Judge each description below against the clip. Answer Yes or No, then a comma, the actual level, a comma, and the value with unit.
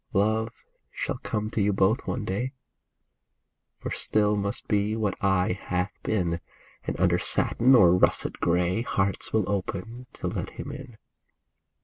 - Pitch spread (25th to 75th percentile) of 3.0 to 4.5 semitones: No, narrow, 2.6 semitones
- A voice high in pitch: No, low, 105 Hz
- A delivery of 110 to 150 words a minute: Yes, average, 145 wpm